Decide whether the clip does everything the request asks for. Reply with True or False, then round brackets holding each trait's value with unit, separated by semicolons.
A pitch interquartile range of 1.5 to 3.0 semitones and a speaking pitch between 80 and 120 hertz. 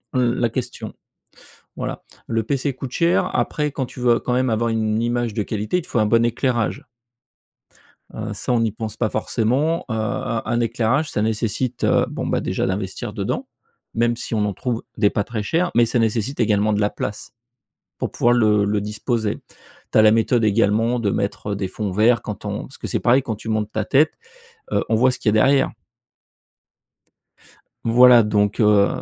True (2.5 semitones; 115 Hz)